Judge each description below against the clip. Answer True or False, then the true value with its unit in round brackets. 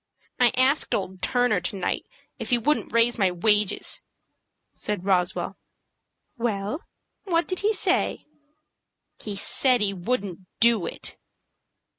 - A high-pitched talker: True (215 Hz)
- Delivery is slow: True (125 wpm)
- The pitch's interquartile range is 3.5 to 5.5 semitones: True (4.6 semitones)